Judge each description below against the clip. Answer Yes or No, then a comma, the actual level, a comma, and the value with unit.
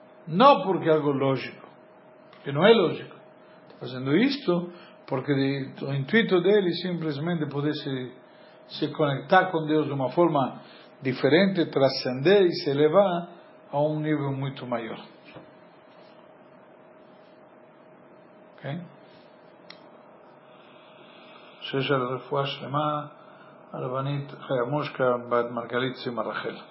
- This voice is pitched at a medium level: Yes, medium, 145 Hz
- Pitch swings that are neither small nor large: Yes, average, 3.7 semitones